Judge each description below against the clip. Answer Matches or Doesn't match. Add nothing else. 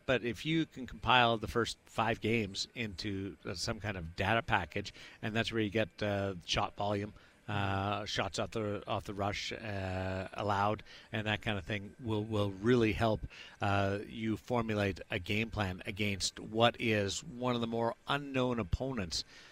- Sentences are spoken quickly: Doesn't match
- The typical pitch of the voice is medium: Doesn't match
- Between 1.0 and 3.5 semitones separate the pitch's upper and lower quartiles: Matches